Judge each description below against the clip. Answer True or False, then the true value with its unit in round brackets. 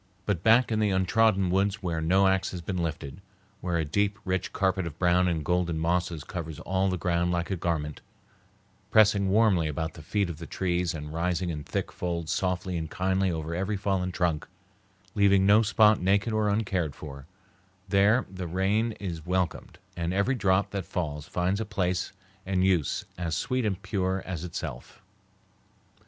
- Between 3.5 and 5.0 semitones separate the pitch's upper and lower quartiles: False (2.7 semitones)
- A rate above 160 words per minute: True (175 wpm)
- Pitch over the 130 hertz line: False (90 Hz)